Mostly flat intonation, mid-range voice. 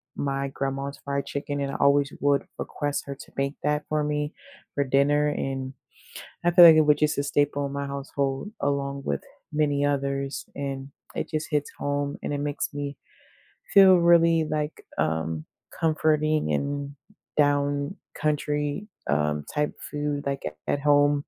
Yes: narrow, 1.2 semitones; medium, 145 Hz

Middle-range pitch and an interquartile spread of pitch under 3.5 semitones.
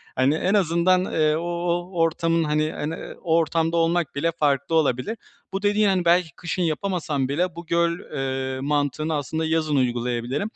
Yes: medium, 160 Hz; average, 3.0 semitones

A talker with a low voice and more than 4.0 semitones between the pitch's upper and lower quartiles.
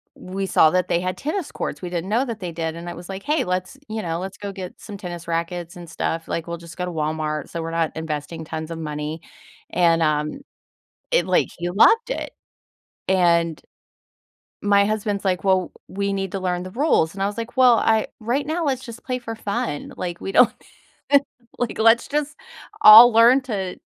No: medium, 185 Hz; average, 4.8 semitones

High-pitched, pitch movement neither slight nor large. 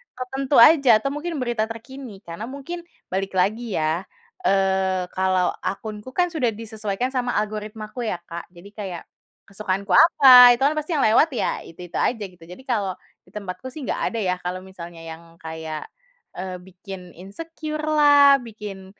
No: high, 210 Hz; wide, 5.9 semitones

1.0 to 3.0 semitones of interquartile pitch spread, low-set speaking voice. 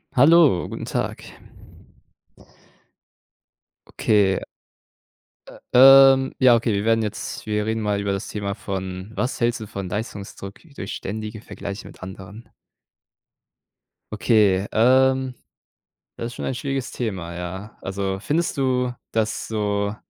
No: average, 4.0 semitones; low, 110 Hz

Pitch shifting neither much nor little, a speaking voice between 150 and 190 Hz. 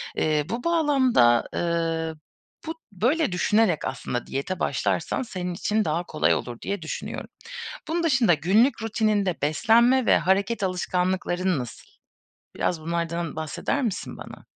No: wide, 5.9 semitones; medium, 185 Hz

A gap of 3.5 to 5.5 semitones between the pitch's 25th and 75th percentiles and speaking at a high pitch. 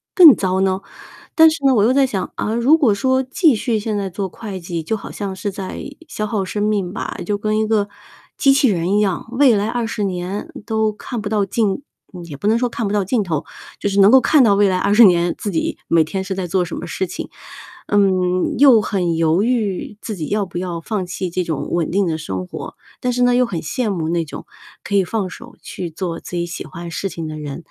Yes: average, 3.9 semitones; high, 200 Hz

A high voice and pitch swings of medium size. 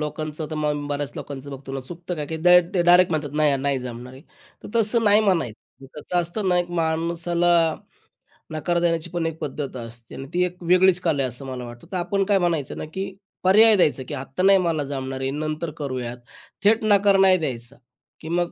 No: medium, 160 Hz; average, 4.7 semitones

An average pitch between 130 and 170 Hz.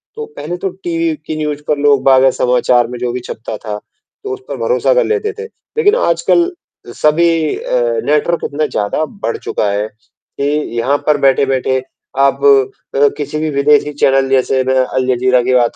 Yes: medium, 140 Hz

